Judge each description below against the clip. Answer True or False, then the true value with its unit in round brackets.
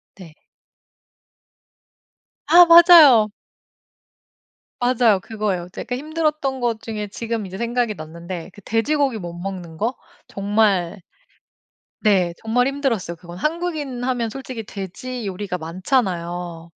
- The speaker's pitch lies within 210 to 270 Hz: True (220 Hz)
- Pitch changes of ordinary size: False (5.7 semitones)